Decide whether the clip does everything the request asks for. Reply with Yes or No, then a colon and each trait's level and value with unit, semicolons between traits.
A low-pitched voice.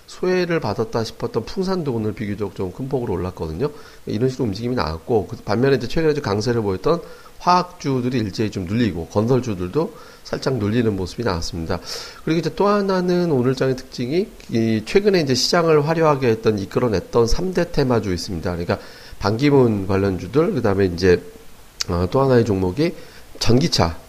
Yes: low, 115 Hz